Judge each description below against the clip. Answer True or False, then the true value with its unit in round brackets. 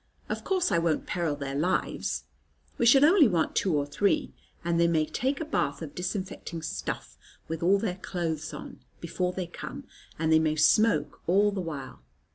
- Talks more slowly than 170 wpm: False (185 wpm)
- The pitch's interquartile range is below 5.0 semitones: True (4.1 semitones)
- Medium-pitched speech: True (170 Hz)